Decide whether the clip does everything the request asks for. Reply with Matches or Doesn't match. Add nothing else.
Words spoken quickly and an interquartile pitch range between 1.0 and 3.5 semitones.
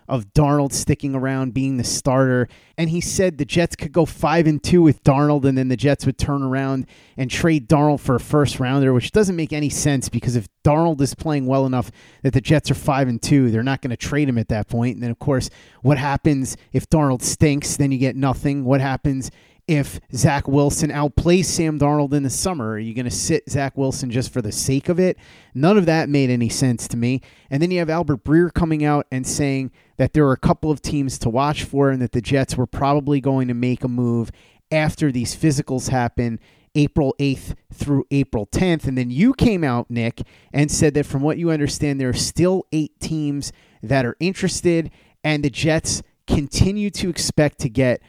Matches